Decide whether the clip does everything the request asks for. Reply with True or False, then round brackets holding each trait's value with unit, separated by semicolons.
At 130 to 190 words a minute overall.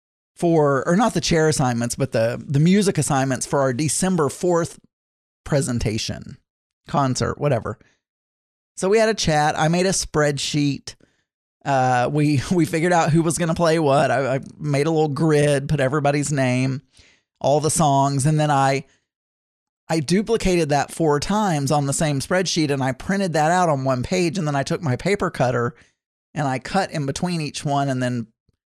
True (175 wpm)